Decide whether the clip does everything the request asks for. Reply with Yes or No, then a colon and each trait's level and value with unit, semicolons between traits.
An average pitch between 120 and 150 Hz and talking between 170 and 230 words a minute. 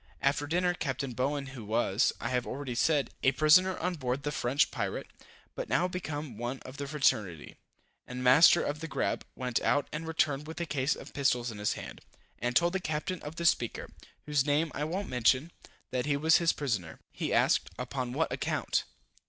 Yes: medium, 140 Hz; average, 195 wpm